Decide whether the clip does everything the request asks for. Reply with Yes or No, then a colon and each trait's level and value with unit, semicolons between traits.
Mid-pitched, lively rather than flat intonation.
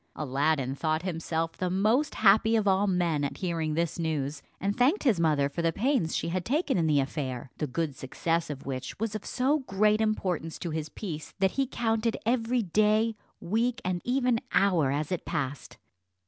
Yes: medium, 180 Hz; wide, 6.1 semitones